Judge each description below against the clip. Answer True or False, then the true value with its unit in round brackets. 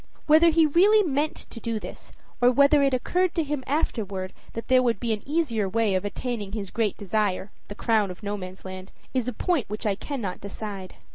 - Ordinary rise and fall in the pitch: False (5.8 semitones)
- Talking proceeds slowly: False (200 wpm)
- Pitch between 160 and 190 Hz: False (230 Hz)